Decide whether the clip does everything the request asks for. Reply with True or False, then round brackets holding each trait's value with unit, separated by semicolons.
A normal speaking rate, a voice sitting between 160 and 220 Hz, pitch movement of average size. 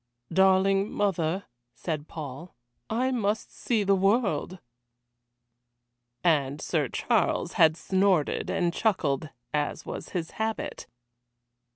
False (100 wpm; 185 Hz; 4.3 semitones)